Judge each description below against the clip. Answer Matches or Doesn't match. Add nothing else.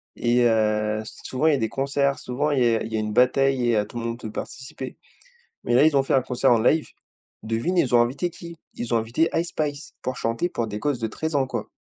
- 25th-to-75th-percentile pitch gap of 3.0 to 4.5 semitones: Matches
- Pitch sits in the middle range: Doesn't match